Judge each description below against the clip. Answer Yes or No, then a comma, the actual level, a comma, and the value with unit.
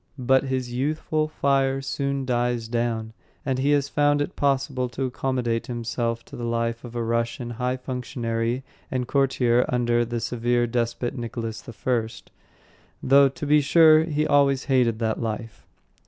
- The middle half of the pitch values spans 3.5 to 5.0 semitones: No, average, 2.7 semitones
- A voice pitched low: Yes, low, 125 Hz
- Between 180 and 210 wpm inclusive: No, average, 150 wpm